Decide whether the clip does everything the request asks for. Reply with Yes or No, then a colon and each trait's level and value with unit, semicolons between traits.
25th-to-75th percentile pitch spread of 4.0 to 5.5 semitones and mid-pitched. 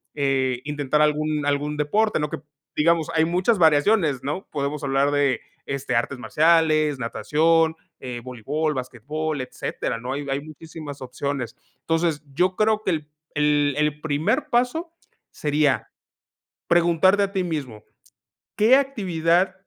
No: average, 3.2 semitones; medium, 150 Hz